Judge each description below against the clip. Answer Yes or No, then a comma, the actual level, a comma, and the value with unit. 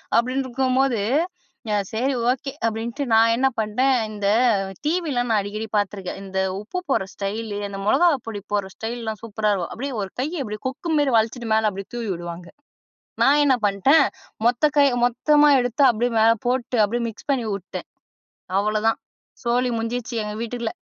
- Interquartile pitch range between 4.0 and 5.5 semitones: No, average, 3.6 semitones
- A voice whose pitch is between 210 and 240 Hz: Yes, high, 230 Hz